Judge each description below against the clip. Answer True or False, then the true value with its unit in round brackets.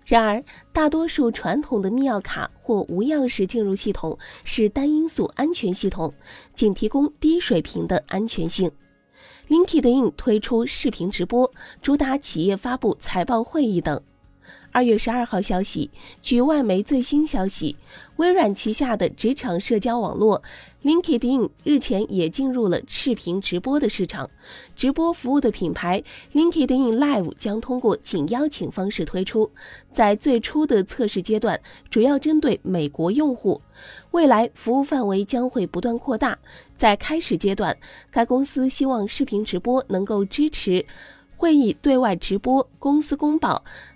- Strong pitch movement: True (5.9 semitones)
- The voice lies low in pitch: False (235 Hz)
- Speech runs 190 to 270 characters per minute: True (260 characters per minute)